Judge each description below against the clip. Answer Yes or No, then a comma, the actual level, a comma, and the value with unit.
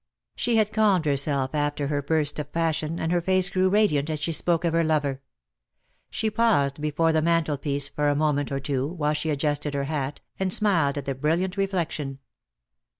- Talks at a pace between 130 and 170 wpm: No, average, 190 wpm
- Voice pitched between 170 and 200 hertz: No, medium, 155 Hz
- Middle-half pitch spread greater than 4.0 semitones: No, average, 3.3 semitones